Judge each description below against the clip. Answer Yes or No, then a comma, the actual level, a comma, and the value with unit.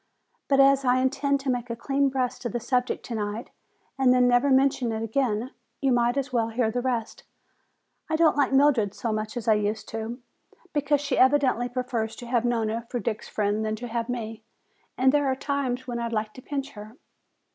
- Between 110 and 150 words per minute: No, fast, 205 wpm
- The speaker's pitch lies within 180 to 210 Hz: No, high, 245 Hz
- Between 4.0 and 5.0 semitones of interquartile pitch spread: No, average, 3.1 semitones